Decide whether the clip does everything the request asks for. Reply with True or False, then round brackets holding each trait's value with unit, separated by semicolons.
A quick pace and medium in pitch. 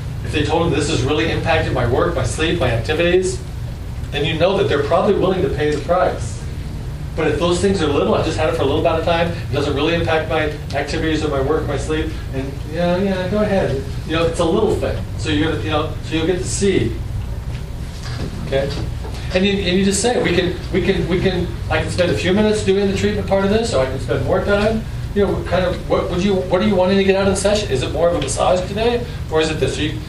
True (265 wpm; 170 Hz)